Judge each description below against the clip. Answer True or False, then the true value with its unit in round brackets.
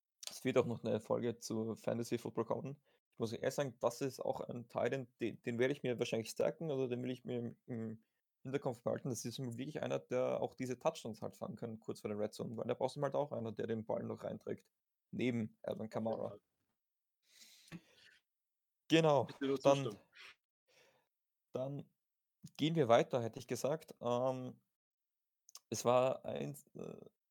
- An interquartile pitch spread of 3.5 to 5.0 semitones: False (2.9 semitones)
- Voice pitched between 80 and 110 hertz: False (125 Hz)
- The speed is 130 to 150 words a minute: False (180 wpm)